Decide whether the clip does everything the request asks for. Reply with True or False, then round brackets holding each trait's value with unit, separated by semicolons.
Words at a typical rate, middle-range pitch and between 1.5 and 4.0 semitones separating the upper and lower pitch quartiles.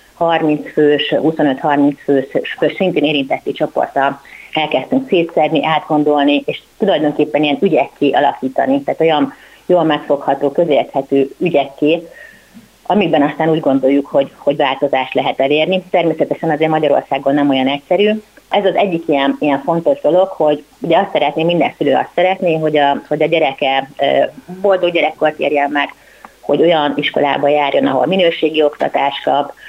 True (140 wpm; 150 Hz; 2.6 semitones)